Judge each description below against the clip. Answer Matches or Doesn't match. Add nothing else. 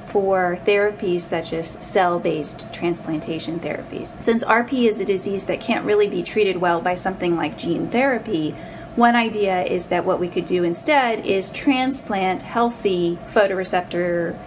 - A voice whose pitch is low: Doesn't match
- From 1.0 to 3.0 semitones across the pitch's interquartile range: Doesn't match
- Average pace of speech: Matches